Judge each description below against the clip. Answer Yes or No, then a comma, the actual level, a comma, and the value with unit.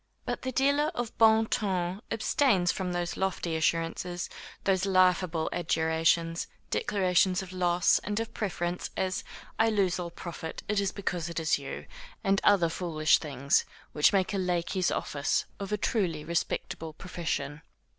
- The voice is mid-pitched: Yes, medium, 180 Hz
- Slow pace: No, average, 150 wpm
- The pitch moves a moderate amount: Yes, average, 3.0 semitones